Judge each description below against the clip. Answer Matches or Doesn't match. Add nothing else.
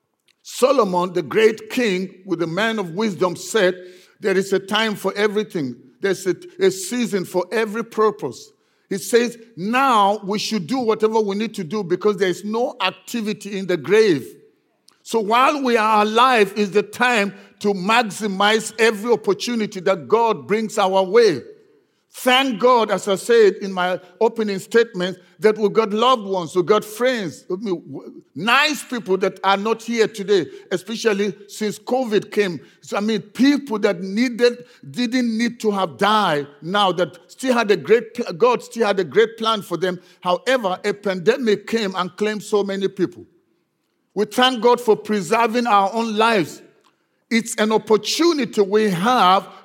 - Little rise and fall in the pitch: Doesn't match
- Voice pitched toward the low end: Doesn't match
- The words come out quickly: Doesn't match